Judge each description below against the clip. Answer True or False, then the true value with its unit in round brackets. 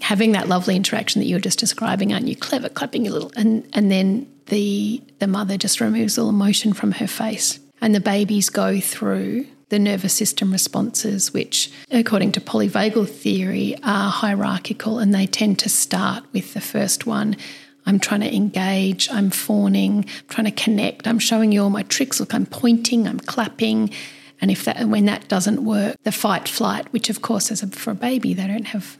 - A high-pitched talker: True (210 Hz)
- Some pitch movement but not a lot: False (1.9 semitones)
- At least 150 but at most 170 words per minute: False (200 wpm)